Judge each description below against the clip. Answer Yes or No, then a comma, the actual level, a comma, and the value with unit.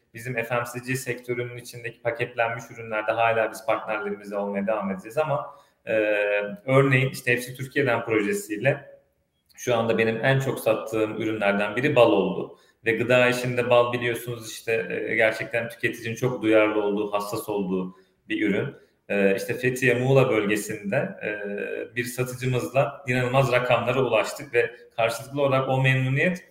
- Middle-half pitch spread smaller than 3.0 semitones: Yes, narrow, 2.6 semitones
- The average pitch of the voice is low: Yes, low, 120 Hz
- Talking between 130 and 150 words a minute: Yes, fast, 140 wpm